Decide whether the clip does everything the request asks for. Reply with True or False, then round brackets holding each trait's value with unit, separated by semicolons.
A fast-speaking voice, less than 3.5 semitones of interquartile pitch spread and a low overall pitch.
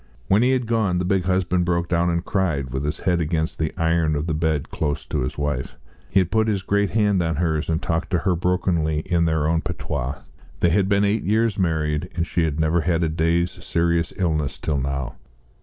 True (220 wpm; 2.8 semitones; 85 Hz)